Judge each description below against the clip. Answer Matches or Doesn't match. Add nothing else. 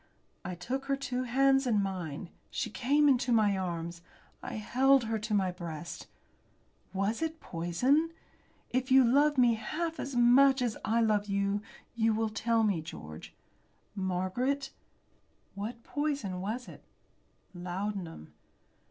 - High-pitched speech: Matches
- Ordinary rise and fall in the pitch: Doesn't match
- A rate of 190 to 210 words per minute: Doesn't match